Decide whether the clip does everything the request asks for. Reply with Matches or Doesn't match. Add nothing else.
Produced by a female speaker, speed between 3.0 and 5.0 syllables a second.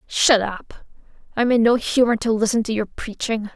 Matches